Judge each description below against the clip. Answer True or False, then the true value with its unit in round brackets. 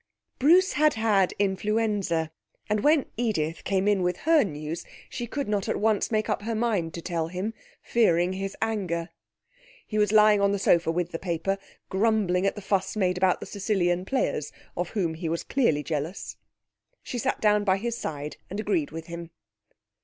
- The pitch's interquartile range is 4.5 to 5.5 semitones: False (4.0 semitones)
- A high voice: True (195 Hz)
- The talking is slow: False (185 wpm)